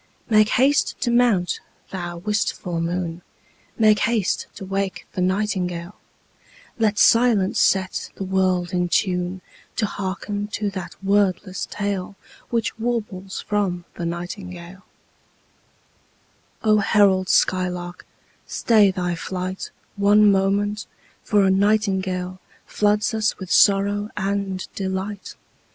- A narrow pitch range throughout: Yes, narrow, 2.2 semitones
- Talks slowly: Yes, slow, 110 wpm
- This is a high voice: Yes, high, 195 Hz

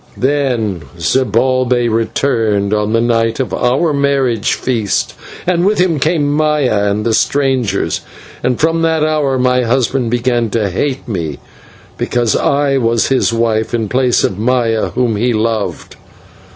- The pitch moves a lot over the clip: No, average, 3.5 semitones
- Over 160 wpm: No, average, 145 wpm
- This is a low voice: Yes, low, 125 Hz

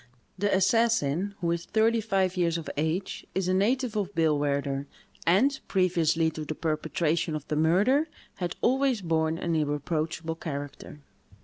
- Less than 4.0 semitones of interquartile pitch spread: No, average, 4.4 semitones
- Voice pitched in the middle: Yes, medium, 170 Hz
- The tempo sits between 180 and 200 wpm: No, average, 145 wpm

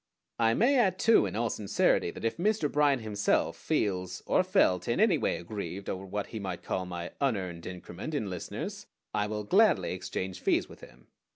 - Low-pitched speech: Yes, low, 105 Hz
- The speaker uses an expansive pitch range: Yes, wide, 7.9 semitones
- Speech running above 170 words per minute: Yes, average, 190 wpm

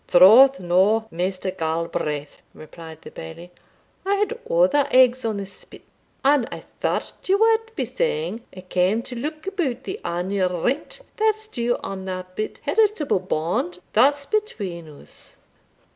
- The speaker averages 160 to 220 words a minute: No, average, 145 wpm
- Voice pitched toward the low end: No, high, 225 Hz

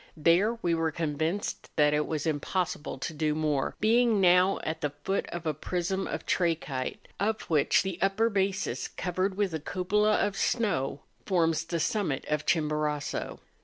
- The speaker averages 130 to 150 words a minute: No, average, 165 wpm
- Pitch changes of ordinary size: Yes, average, 4.2 semitones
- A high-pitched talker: No, medium, 170 Hz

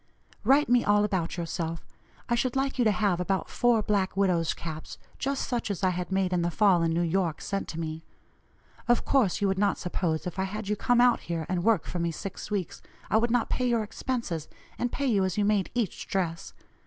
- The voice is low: No, high, 195 Hz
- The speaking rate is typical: No, fast, 230 wpm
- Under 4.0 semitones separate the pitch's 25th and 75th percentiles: No, average, 4.9 semitones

